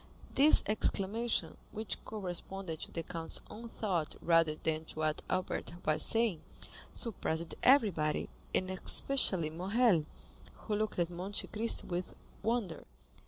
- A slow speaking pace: Yes, slow, 125 wpm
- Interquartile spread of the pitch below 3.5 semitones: No, average, 4.8 semitones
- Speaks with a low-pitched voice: No, medium, 185 Hz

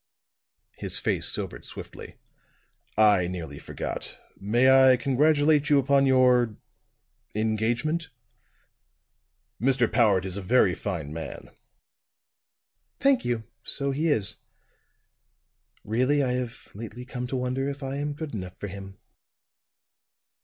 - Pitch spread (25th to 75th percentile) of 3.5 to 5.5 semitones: Yes, average, 4.9 semitones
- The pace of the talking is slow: Yes, slow, 115 wpm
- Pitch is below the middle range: Yes, low, 125 Hz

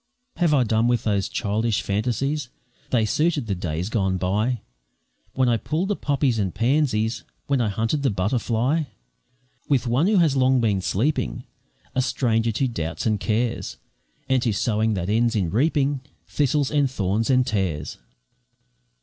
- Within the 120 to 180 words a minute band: Yes, average, 160 wpm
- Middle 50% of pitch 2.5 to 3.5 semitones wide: No, average, 4.6 semitones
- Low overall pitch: Yes, low, 115 Hz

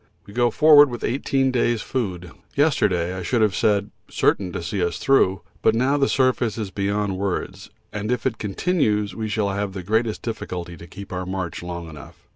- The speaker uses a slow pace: No, average, 195 wpm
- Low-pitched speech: Yes, low, 105 Hz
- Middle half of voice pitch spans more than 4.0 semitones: Yes, average, 4.5 semitones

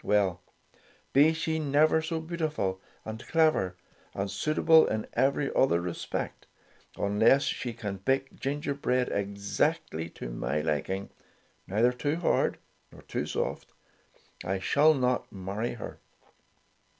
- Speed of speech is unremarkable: No, slow, 120 wpm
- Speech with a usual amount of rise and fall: No, wide, 7.3 semitones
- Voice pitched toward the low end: Yes, low, 120 Hz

